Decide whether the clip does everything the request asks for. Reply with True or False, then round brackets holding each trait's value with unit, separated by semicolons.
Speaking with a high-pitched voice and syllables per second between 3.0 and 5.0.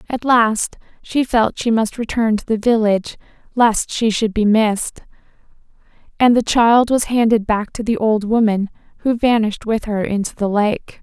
True (220 Hz; 4.7 syllables/s)